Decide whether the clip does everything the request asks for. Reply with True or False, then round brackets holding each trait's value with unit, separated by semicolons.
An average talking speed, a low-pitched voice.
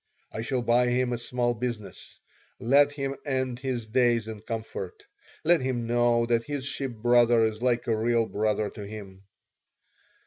True (165 wpm; 120 Hz)